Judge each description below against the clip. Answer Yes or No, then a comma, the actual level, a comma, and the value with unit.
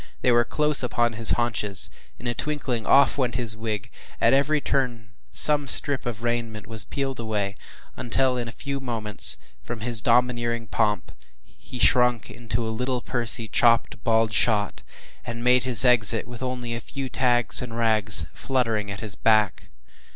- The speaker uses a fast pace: No, average, 165 wpm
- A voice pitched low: Yes, low, 120 Hz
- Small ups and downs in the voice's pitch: Yes, narrow, 2.1 semitones